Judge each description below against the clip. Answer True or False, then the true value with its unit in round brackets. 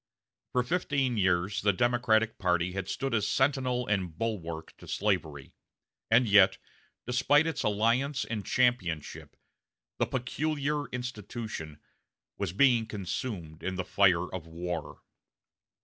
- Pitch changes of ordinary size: False (5.7 semitones)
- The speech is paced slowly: True (120 wpm)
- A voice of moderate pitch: False (105 Hz)